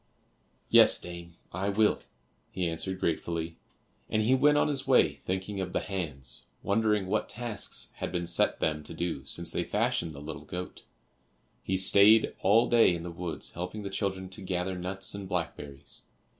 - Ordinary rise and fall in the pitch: Yes, average, 3.2 semitones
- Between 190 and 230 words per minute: No, average, 170 wpm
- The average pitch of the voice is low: Yes, very low, 95 Hz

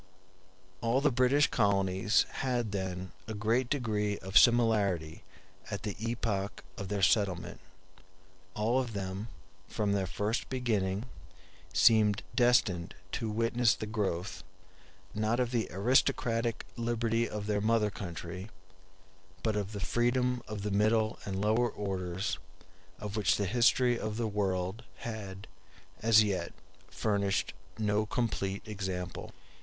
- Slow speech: Yes, slow, 130 wpm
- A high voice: No, low, 105 Hz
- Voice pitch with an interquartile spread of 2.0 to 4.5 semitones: Yes, average, 2.9 semitones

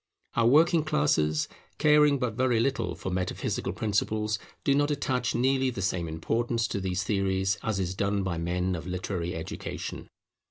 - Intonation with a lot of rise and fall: Yes, wide, 6.0 semitones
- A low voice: Yes, low, 105 Hz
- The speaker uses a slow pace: No, average, 160 wpm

